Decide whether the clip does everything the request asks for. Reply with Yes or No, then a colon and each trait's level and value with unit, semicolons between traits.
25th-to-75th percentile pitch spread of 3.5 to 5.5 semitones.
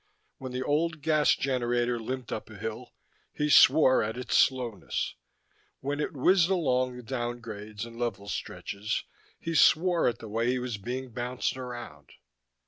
No: average, 2.9 semitones